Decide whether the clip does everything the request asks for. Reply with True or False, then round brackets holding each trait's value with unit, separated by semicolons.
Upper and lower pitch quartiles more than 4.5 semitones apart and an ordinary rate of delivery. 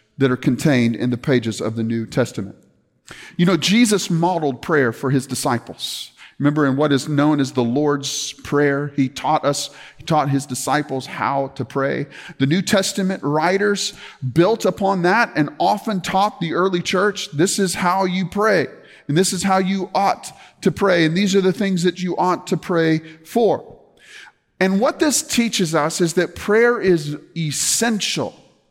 True (5.4 semitones; 175 wpm)